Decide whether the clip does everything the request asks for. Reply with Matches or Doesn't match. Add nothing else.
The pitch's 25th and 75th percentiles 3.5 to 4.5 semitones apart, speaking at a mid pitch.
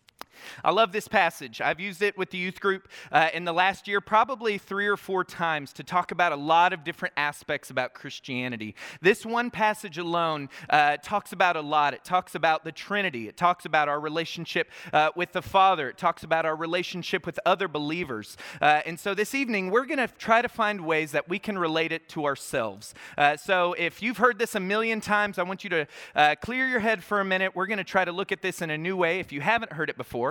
Matches